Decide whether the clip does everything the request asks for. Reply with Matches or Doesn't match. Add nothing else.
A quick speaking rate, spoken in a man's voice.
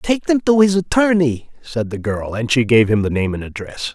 Matches